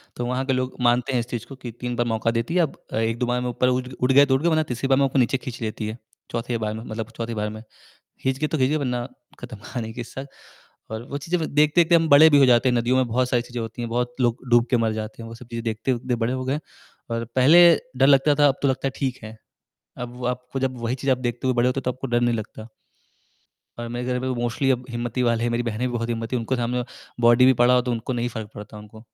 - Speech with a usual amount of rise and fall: No, narrow, 2.0 semitones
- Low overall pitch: Yes, low, 125 Hz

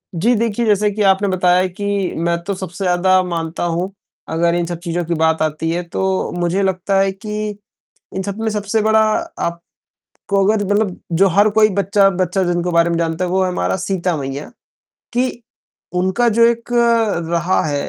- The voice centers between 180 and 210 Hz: Yes, medium, 185 Hz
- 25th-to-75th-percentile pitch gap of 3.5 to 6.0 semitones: No, average, 3.0 semitones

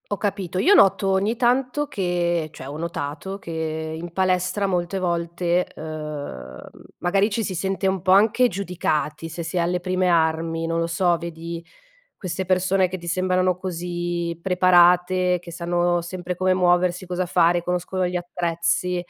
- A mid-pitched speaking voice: Yes, medium, 180 Hz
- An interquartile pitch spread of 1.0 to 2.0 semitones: Yes, narrow, 1.7 semitones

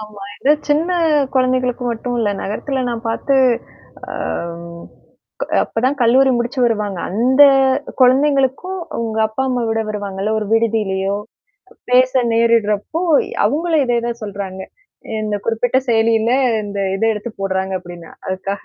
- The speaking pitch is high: Yes, high, 230 Hz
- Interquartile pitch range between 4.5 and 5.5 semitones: No, average, 3.8 semitones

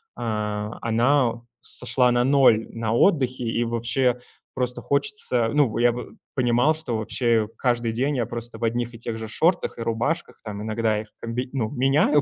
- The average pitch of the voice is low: Yes, low, 120 Hz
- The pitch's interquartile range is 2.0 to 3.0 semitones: Yes, narrow, 2.4 semitones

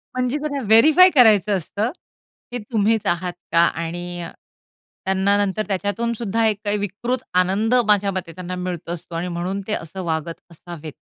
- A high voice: Yes, high, 195 Hz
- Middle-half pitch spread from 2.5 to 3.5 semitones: No, average, 4.0 semitones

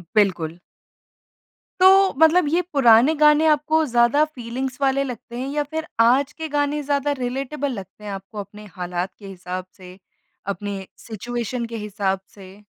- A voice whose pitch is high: Yes, high, 240 Hz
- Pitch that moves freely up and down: Yes, wide, 6.4 semitones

